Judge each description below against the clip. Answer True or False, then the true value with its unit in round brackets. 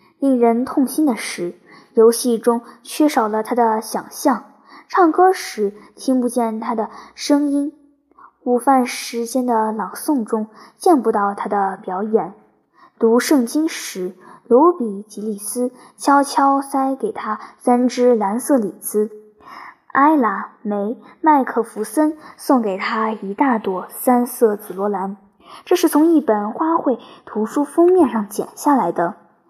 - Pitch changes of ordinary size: True (4.8 semitones)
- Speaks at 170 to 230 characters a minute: True (195 characters per minute)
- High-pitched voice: True (240 Hz)